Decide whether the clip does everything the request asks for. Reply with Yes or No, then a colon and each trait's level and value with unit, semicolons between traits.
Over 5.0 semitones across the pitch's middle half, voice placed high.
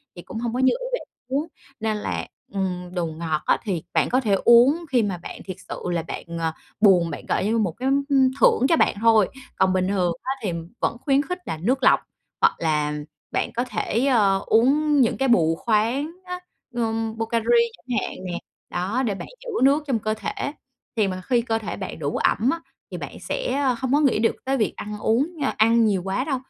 Yes: wide, 5.5 semitones; high, 225 Hz